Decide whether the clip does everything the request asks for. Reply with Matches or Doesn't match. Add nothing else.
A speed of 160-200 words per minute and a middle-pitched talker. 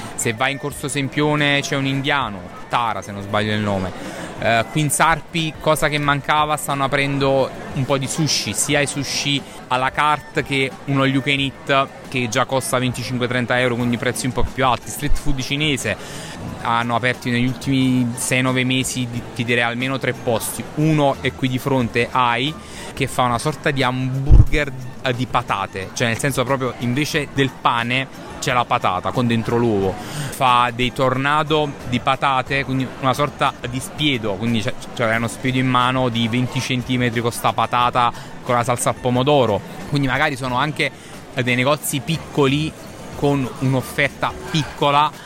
Doesn't match